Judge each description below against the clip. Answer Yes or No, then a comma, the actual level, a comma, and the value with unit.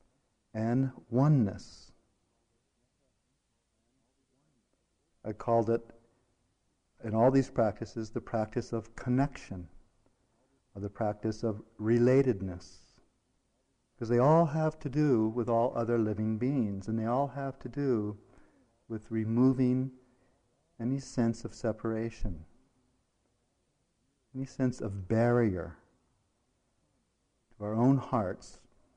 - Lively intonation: No, average, 2.8 semitones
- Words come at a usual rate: No, slow, 100 wpm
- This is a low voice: Yes, low, 115 Hz